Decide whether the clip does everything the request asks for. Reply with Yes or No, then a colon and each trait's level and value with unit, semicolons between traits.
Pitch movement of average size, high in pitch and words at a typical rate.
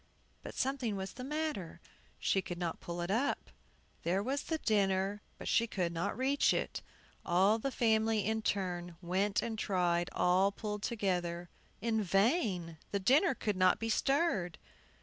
Yes: average, 4.4 semitones; high, 200 Hz; average, 160 wpm